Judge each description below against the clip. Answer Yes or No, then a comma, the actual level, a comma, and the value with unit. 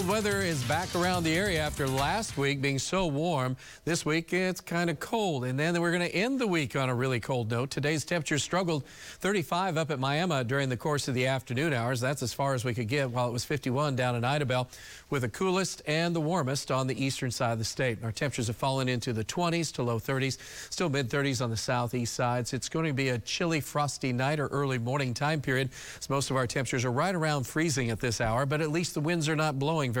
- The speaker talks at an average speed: No, fast, 250 wpm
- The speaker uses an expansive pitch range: No, average, 4.0 semitones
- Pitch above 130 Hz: Yes, medium, 140 Hz